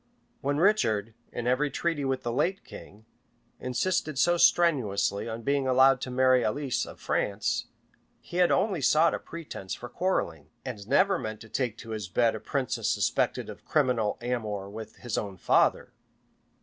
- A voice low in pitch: Yes, low, 125 Hz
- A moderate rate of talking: Yes, average, 170 wpm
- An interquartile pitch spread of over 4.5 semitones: Yes, average, 5.3 semitones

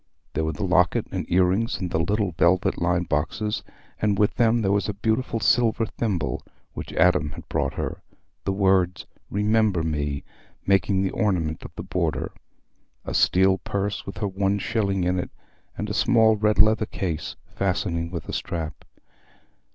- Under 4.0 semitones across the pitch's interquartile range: Yes, average, 3.2 semitones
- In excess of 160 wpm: Yes, average, 170 wpm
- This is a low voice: Yes, very low, 95 Hz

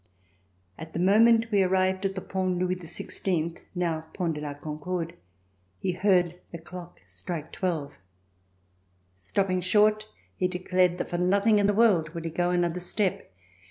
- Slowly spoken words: No, average, 160 wpm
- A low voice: No, medium, 180 Hz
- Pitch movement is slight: Yes, narrow, 2.3 semitones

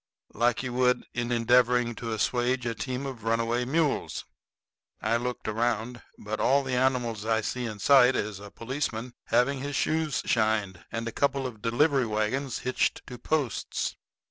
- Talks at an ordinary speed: Yes, average, 165 wpm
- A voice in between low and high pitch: No, low, 120 Hz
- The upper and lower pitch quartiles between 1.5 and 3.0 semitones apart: Yes, narrow, 2.5 semitones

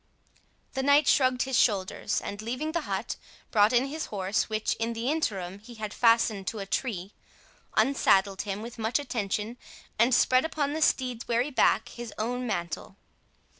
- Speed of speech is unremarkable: Yes, average, 170 wpm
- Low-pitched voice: No, high, 230 Hz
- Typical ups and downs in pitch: Yes, average, 3.8 semitones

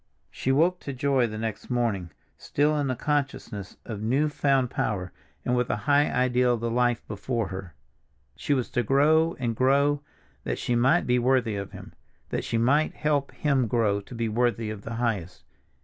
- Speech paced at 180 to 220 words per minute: Yes, average, 185 wpm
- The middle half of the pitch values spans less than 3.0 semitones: No, average, 3.7 semitones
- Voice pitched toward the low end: Yes, low, 125 Hz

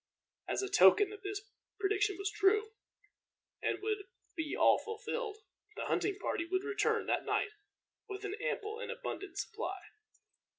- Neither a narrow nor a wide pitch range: No, narrow, 1.6 semitones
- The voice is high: Yes, very high, 410 Hz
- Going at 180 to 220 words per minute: No, average, 145 wpm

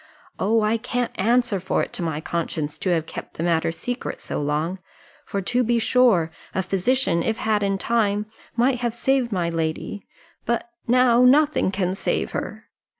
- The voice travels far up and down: Yes, wide, 5.9 semitones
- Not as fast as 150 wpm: No, average, 175 wpm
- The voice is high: Yes, high, 205 Hz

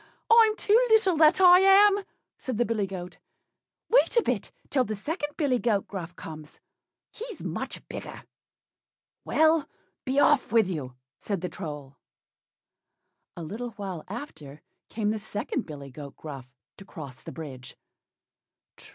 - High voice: Yes, high, 215 Hz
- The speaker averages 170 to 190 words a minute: No, average, 145 wpm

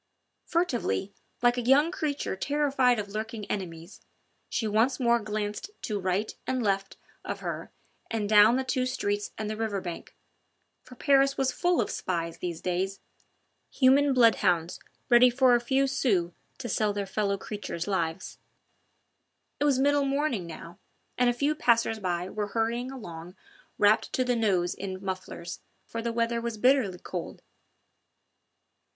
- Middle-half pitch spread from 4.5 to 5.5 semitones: Yes, average, 4.8 semitones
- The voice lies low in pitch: No, high, 220 Hz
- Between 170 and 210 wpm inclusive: No, average, 155 wpm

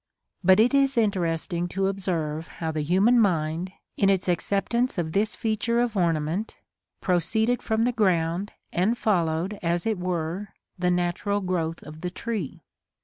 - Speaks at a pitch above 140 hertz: Yes, medium, 185 Hz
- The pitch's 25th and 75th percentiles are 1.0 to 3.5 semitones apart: No, average, 4.3 semitones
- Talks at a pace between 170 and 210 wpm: No, average, 150 wpm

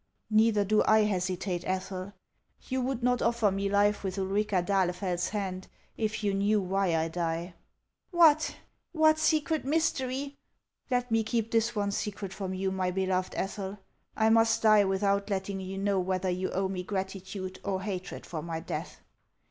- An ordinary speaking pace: Yes, average, 170 wpm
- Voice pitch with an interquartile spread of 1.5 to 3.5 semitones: Yes, average, 2.8 semitones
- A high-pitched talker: Yes, high, 200 Hz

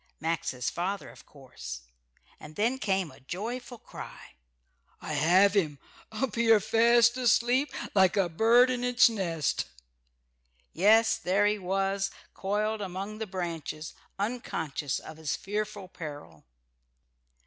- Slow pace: Yes, slow, 125 wpm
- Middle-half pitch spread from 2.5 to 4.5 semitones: No, wide, 5.4 semitones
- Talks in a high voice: Yes, high, 195 Hz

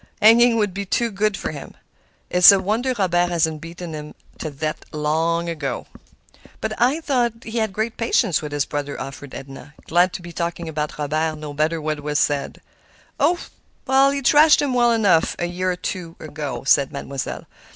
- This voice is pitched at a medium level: Yes, medium, 170 Hz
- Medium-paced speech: Yes, average, 180 wpm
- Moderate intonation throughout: No, wide, 6.0 semitones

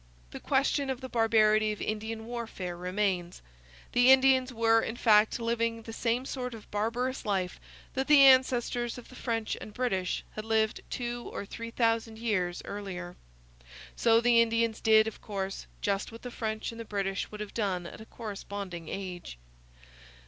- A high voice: Yes, high, 225 Hz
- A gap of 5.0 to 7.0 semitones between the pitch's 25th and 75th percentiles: No, average, 2.8 semitones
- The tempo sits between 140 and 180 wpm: Yes, average, 170 wpm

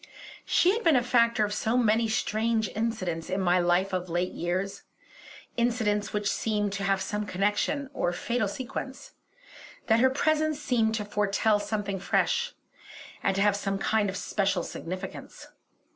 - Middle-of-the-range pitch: No, high, 210 Hz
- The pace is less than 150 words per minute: No, average, 160 wpm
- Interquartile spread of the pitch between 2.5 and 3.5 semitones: Yes, average, 3.2 semitones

